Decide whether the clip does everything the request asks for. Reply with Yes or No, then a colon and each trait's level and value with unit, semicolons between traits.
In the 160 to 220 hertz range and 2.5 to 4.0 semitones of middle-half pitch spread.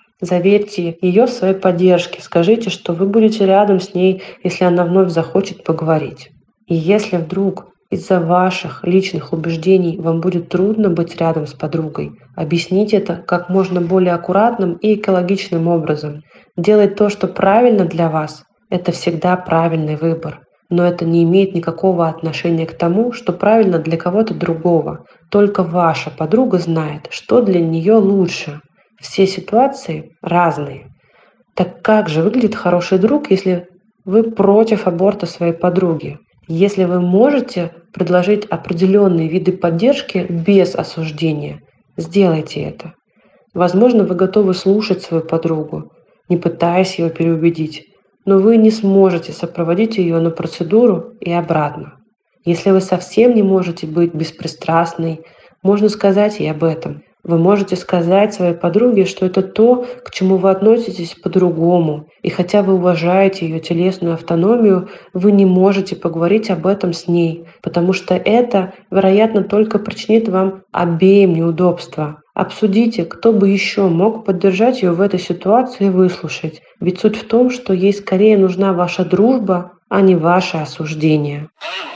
Yes: medium, 185 Hz; average, 2.8 semitones